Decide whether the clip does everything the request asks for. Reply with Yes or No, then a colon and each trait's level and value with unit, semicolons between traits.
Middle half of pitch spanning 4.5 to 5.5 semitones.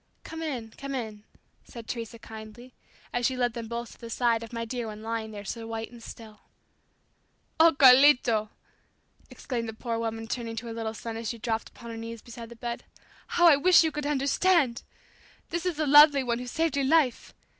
No: average, 3.4 semitones